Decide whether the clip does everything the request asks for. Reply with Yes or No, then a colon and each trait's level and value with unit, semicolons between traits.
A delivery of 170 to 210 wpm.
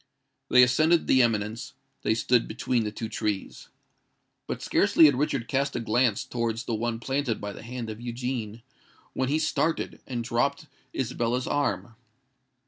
No: average, 155 wpm